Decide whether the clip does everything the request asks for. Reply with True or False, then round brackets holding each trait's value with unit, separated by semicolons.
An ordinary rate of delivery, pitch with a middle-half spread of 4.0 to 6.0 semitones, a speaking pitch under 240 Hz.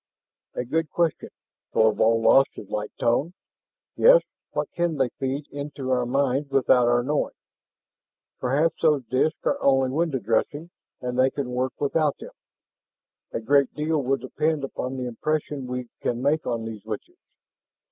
False (155 wpm; 3.3 semitones; 135 Hz)